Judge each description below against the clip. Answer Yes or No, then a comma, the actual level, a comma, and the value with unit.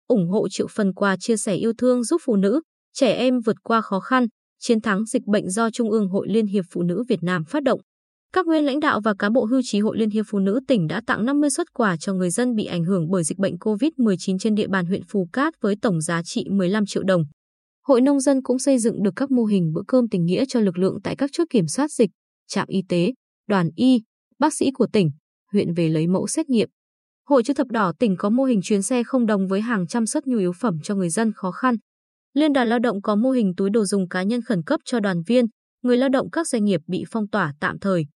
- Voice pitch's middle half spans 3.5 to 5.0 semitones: Yes, average, 4.7 semitones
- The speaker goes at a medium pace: No, fast, 260 wpm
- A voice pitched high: Yes, high, 220 Hz